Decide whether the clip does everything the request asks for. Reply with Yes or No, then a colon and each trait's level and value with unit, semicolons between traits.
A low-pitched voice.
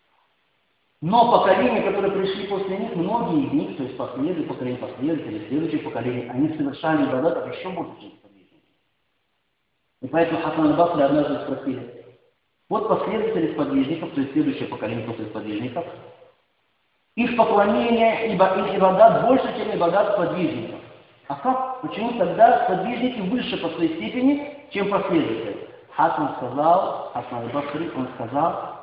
No: high, 190 Hz